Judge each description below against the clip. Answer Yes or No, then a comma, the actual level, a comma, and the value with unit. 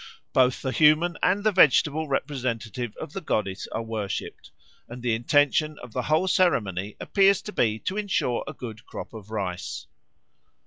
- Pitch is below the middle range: Yes, low, 125 Hz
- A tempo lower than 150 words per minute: No, average, 165 wpm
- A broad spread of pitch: Yes, wide, 6.0 semitones